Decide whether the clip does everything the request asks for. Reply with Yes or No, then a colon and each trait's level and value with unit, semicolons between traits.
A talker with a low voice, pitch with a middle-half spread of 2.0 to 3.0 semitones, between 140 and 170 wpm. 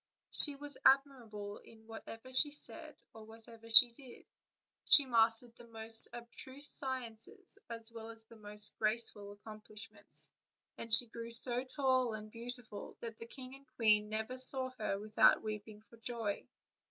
No: high, 230 Hz; average, 2.7 semitones; average, 155 wpm